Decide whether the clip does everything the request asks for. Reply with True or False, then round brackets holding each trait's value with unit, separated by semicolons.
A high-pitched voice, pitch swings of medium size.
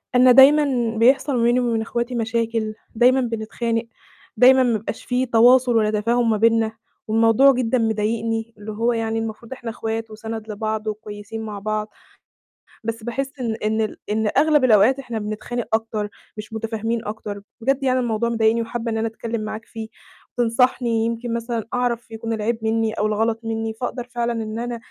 False (225 Hz; 1.6 semitones)